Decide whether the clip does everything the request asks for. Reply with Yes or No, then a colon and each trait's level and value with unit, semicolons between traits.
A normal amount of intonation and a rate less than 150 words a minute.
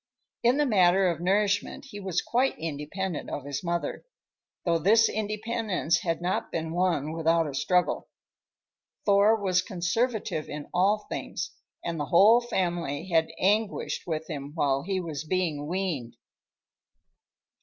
Yes: average, 4.1 semitones; average, 140 wpm